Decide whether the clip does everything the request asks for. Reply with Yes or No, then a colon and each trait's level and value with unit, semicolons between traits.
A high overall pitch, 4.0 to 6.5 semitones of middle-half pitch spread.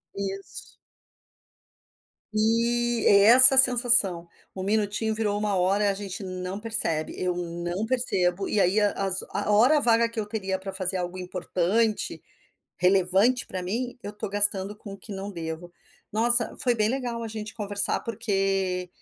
No: high, 205 Hz; average, 3.3 semitones